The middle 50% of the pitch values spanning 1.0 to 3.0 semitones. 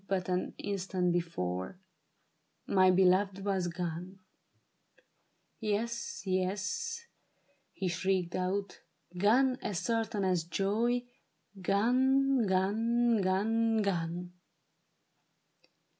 No: average, 3.6 semitones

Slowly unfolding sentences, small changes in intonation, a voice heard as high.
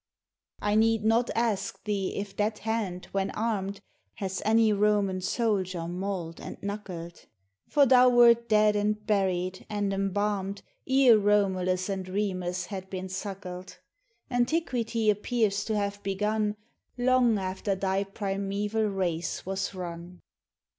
Yes: slow, 125 wpm; narrow, 2.3 semitones; high, 200 Hz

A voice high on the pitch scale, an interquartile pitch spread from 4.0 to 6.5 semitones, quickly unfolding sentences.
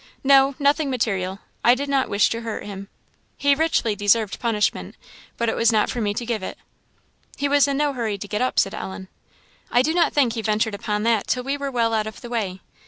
Yes: high, 230 Hz; average, 4.6 semitones; fast, 230 wpm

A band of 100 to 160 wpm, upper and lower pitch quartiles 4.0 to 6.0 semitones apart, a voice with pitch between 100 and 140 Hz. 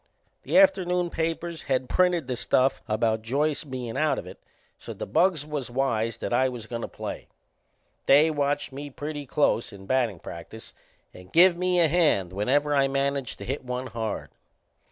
No: average, 175 wpm; average, 4.6 semitones; low, 135 Hz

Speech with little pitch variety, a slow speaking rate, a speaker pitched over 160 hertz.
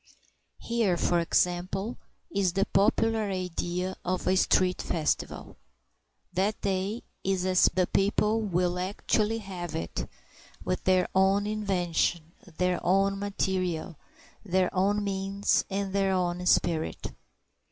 Yes: narrow, 1.8 semitones; slow, 120 wpm; high, 190 Hz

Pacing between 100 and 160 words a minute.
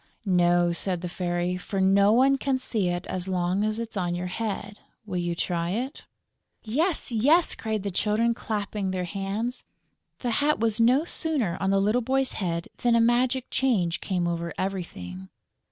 No: average, 175 wpm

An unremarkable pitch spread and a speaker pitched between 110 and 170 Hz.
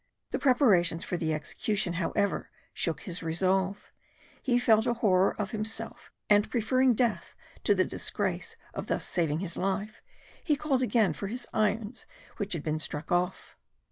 No: average, 4.7 semitones; high, 200 Hz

